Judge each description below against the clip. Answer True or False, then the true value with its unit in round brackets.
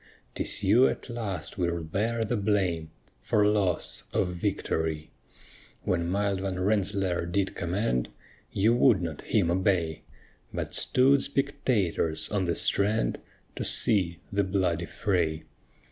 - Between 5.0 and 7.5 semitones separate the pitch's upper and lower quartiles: False (3.5 semitones)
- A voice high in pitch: False (95 Hz)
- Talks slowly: True (130 wpm)